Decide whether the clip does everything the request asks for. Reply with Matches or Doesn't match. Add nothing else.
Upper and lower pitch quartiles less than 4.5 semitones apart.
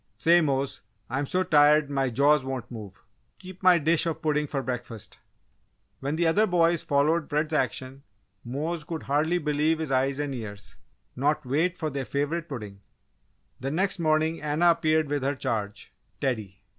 Matches